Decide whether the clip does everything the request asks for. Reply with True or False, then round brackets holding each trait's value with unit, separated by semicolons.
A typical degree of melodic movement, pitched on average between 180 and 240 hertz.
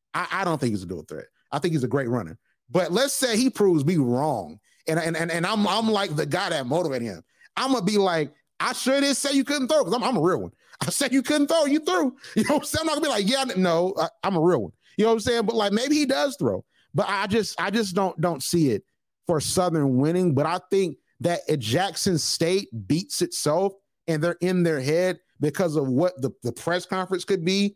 False (6.2 semitones; 185 Hz)